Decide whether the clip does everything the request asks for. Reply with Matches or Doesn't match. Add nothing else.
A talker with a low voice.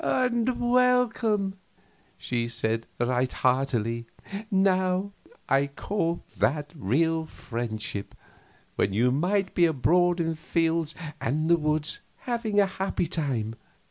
Doesn't match